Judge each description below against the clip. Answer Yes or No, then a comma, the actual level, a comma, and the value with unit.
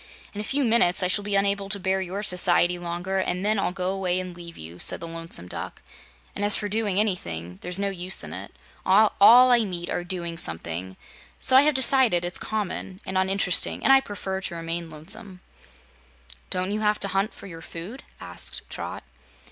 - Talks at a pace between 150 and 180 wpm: No, average, 200 wpm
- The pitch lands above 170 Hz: Yes, high, 190 Hz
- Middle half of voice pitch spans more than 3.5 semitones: No, average, 3.0 semitones